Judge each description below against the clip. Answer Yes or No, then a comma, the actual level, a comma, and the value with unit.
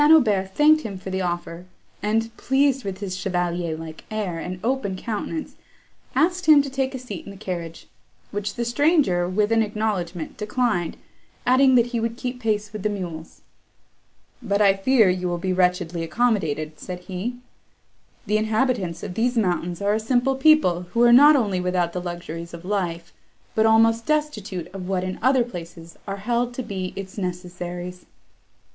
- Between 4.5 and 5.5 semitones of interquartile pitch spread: Yes, average, 5.1 semitones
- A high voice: Yes, high, 200 Hz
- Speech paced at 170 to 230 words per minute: Yes, average, 175 wpm